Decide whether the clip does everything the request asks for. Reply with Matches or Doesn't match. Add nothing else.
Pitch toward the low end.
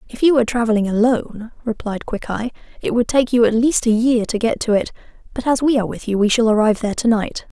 Doesn't match